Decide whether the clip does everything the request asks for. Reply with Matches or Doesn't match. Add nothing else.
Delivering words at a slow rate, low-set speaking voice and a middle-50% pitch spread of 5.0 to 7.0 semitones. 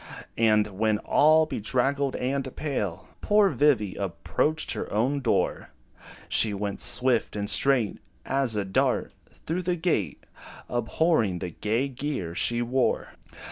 Matches